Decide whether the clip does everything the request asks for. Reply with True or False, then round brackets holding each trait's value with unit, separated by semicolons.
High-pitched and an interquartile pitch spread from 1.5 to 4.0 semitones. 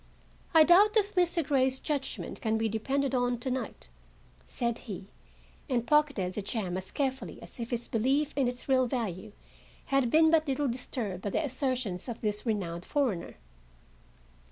False (250 Hz; 4.4 semitones)